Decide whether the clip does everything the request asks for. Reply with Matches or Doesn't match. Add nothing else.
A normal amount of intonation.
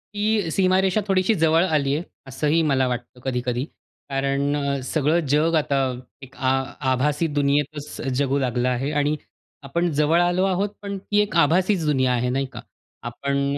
Matches